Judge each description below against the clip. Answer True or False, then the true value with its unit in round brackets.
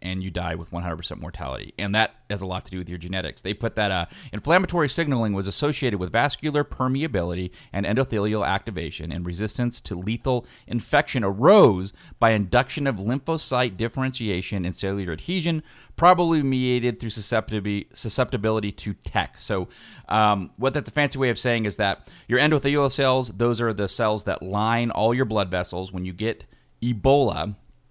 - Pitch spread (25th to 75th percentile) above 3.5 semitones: True (5.1 semitones)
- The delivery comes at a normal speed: True (170 wpm)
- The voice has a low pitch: True (110 Hz)